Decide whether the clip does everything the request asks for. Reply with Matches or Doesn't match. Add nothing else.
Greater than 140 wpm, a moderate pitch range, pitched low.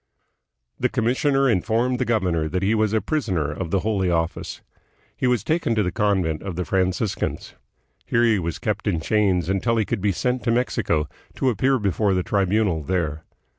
Matches